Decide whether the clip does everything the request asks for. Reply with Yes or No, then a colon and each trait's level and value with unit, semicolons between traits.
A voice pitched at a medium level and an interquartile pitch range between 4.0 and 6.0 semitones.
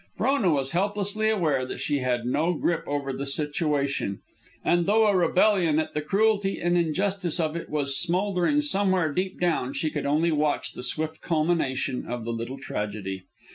Yes: medium, 160 Hz; average, 5.3 semitones